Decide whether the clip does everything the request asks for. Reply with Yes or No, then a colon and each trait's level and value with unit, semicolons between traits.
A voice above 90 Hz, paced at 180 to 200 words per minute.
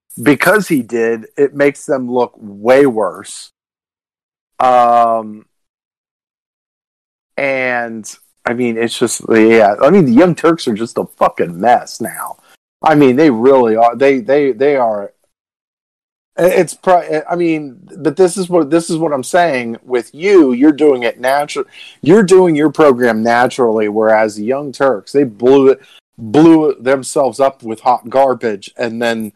No: low, 135 Hz; average, 155 wpm